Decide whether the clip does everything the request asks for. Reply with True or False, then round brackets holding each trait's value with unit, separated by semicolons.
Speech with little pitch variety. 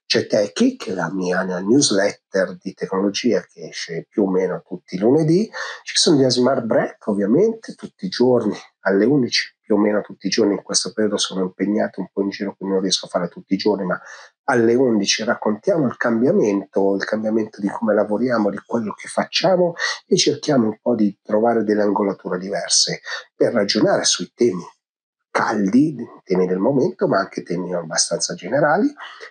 False (3.9 semitones)